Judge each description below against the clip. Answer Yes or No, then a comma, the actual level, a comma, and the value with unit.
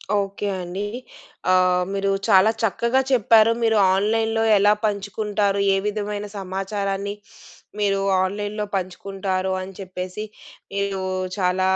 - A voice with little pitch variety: Yes, narrow, 1.6 semitones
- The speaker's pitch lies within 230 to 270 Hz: No, high, 200 Hz